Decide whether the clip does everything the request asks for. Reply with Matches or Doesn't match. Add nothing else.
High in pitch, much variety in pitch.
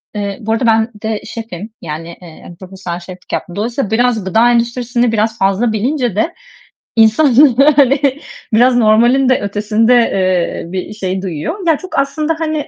Doesn't match